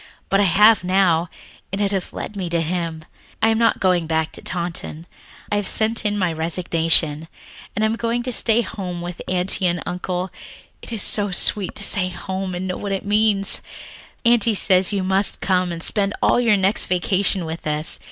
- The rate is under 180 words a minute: No, average, 195 wpm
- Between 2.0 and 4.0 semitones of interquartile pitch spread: Yes, average, 2.9 semitones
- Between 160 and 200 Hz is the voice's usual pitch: Yes, high, 190 Hz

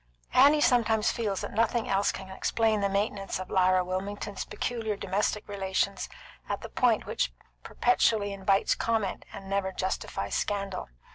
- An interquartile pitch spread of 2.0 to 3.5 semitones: Yes, narrow, 2.4 semitones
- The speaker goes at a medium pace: Yes, average, 145 wpm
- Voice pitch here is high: Yes, high, 200 Hz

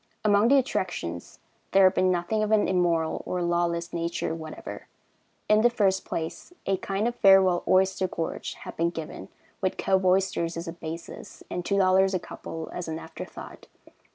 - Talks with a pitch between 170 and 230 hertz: Yes, medium, 185 Hz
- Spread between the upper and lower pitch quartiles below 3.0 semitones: Yes, narrow, 2.4 semitones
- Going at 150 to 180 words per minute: Yes, average, 175 wpm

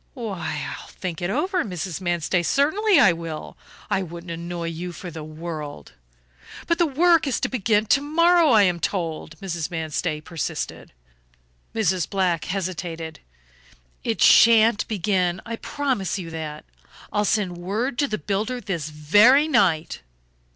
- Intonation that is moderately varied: No, wide, 5.7 semitones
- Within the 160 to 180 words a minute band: No, average, 150 wpm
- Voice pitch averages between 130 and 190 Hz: Yes, medium, 185 Hz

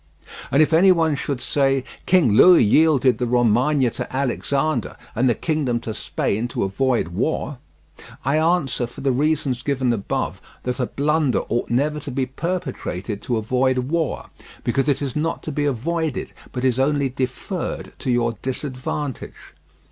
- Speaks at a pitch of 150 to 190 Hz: No, low, 135 Hz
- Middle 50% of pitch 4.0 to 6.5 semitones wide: No, average, 3.6 semitones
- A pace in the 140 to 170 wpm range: Yes, average, 160 wpm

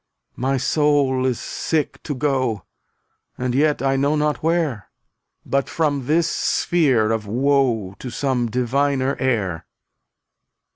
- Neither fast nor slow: No, slow, 130 wpm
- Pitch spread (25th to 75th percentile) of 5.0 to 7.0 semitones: No, average, 3.1 semitones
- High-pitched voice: No, low, 135 Hz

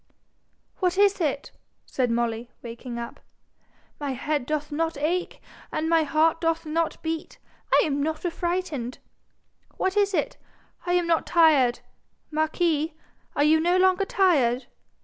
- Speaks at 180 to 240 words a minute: No, average, 145 wpm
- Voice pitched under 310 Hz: No, very high, 315 Hz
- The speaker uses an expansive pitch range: No, average, 3.7 semitones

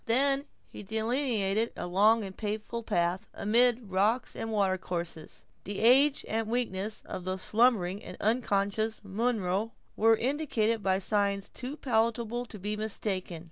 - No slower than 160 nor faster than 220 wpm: No, average, 140 wpm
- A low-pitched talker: No, high, 220 Hz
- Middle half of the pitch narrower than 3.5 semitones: Yes, average, 3.1 semitones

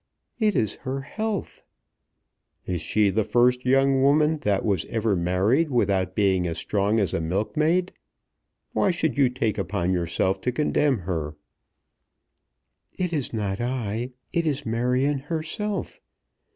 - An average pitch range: No, wide, 6.8 semitones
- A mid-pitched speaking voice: No, low, 120 Hz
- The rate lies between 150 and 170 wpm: No, average, 140 wpm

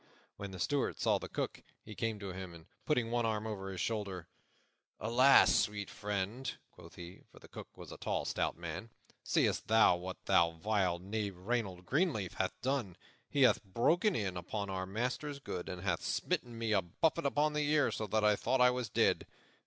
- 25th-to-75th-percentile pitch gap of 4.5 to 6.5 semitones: Yes, average, 4.8 semitones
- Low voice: Yes, low, 105 Hz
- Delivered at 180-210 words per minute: Yes, average, 195 wpm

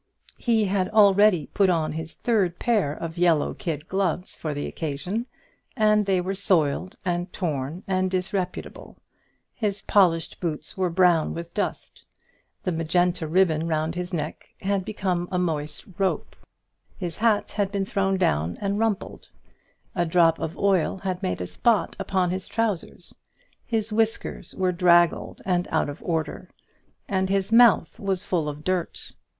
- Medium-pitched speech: Yes, medium, 180 Hz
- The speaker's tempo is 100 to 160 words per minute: Yes, average, 155 wpm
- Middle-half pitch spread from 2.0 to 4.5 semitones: Yes, average, 3.1 semitones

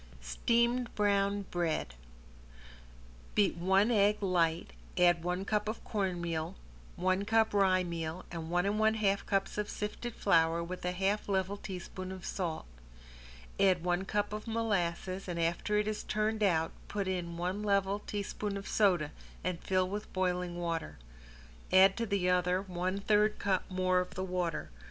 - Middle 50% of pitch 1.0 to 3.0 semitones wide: Yes, narrow, 2.6 semitones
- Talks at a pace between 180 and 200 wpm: No, average, 160 wpm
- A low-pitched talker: No, high, 190 Hz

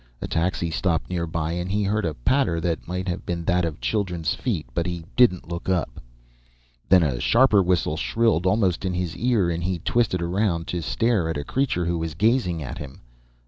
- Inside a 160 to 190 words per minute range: No, average, 200 wpm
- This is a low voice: Yes, very low, 90 Hz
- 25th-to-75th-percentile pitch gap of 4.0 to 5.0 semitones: No, average, 3.1 semitones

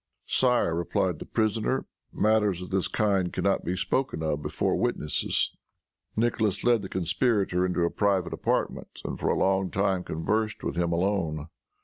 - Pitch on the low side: Yes, very low, 95 Hz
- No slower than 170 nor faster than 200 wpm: No, average, 160 wpm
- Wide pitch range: No, average, 3.6 semitones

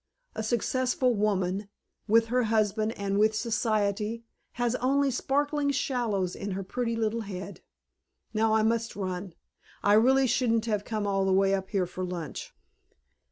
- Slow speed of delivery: No, average, 155 wpm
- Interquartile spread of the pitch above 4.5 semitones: No, average, 3.2 semitones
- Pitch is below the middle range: No, high, 215 Hz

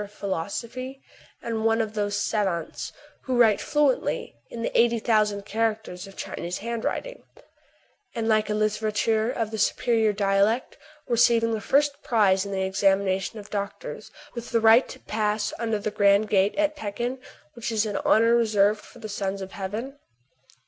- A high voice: Yes, high, 215 Hz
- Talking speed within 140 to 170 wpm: Yes, average, 165 wpm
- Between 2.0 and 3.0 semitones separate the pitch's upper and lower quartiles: Yes, narrow, 2.4 semitones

